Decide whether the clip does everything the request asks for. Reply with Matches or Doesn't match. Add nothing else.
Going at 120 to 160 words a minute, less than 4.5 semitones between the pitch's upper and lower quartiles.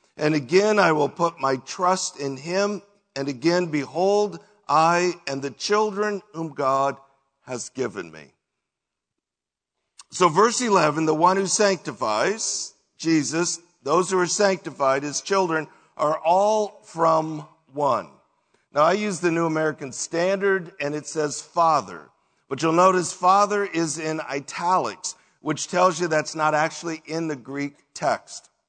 Matches